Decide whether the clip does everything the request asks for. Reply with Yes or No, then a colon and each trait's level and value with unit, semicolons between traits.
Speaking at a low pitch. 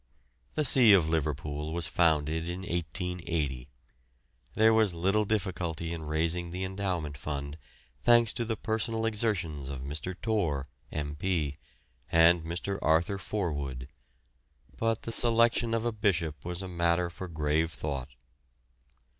Yes: very low, 85 Hz